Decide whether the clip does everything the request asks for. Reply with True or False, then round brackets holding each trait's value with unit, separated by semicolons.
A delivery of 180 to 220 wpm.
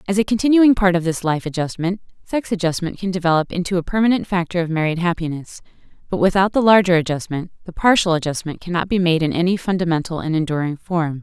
True (190 wpm)